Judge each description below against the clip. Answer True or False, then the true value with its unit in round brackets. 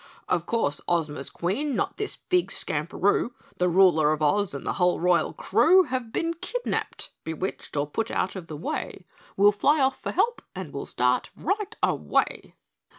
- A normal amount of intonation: False (8.6 semitones)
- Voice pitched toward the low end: False (190 Hz)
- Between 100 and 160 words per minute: False (170 wpm)